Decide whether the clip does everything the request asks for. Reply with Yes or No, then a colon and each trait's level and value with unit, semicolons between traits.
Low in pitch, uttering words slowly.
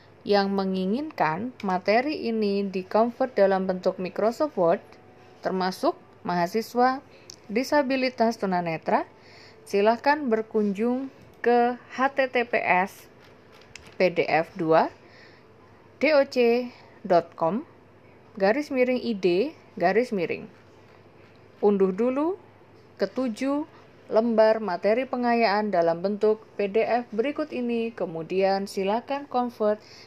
No: high, 220 Hz; slow, 80 wpm